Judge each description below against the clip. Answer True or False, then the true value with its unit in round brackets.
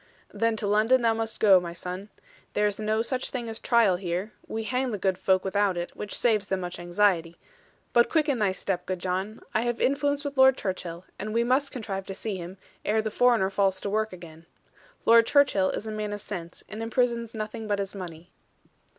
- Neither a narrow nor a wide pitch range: True (3.5 semitones)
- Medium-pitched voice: False (210 Hz)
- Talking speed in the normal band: False (210 wpm)